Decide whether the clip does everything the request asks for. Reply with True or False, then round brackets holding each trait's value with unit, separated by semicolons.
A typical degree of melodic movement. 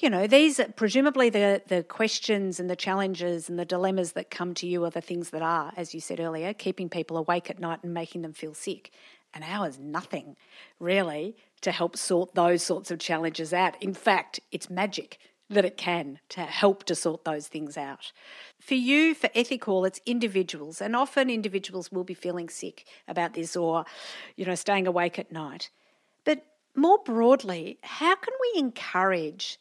True (4.0 semitones)